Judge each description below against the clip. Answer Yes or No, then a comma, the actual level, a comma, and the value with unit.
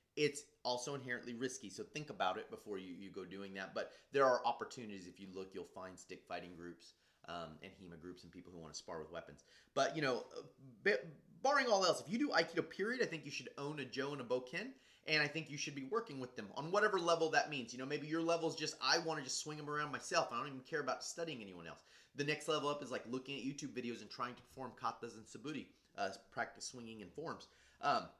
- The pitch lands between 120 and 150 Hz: Yes, low, 135 Hz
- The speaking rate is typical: No, fast, 255 wpm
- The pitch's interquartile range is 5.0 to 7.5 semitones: Yes, average, 5.3 semitones